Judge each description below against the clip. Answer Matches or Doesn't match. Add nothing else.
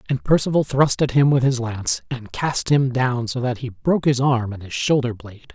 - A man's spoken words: Matches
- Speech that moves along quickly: Matches